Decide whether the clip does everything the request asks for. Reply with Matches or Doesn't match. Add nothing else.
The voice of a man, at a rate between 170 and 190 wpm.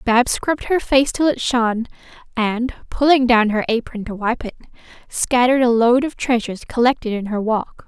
Doesn't match